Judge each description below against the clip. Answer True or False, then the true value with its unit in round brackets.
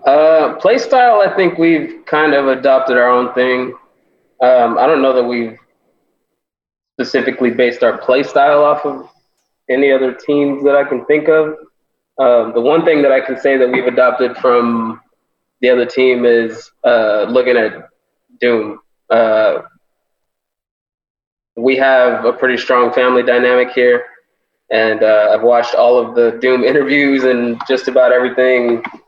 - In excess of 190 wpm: False (155 wpm)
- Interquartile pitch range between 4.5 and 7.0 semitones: False (2.6 semitones)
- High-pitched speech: False (125 Hz)